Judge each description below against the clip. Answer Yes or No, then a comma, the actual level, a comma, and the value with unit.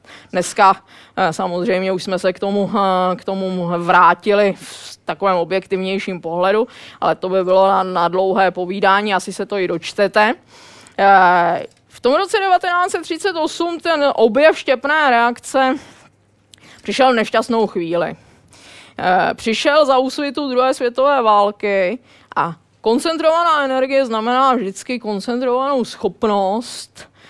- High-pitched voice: Yes, high, 210 Hz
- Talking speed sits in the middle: No, slow, 110 wpm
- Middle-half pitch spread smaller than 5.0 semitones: No, wide, 5.7 semitones